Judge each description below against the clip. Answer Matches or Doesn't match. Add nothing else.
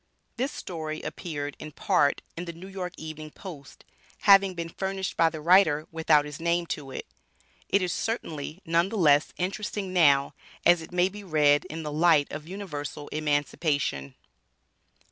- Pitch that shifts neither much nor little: Matches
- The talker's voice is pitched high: Doesn't match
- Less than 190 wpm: Matches